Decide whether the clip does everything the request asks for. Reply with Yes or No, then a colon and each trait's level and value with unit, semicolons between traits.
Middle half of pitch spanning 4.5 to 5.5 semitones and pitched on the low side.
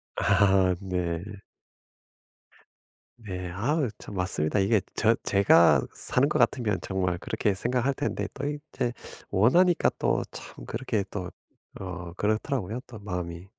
Yes: average, 5.2 semitones; low, 100 Hz